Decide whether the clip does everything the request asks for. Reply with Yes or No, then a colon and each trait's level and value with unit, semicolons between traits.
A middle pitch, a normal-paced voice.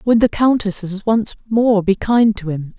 No: high, 210 Hz; average, 195 wpm